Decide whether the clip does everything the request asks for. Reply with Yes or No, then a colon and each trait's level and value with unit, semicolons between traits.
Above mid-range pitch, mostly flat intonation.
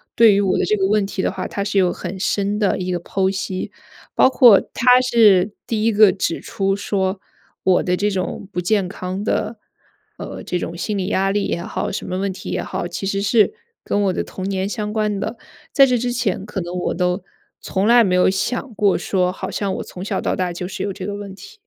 Yes: high, 195 Hz; narrow, 2.1 semitones